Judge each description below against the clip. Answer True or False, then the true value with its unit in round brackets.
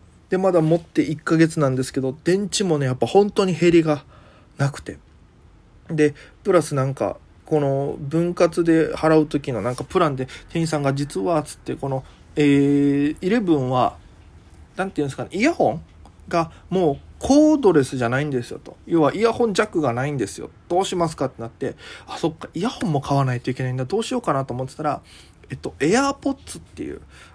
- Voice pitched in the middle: True (150 Hz)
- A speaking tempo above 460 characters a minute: False (375 characters per minute)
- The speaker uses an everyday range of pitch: True (5.0 semitones)